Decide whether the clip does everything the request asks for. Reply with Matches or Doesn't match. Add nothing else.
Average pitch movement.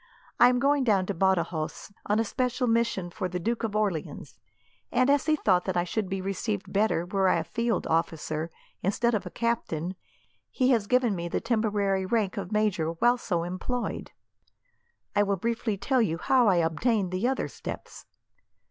Matches